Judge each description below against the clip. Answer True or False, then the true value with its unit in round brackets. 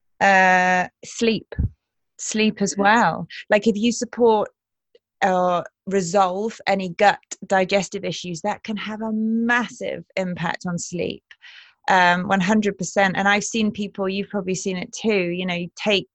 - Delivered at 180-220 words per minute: False (145 wpm)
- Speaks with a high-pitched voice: True (200 Hz)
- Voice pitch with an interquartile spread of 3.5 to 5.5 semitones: False (2.7 semitones)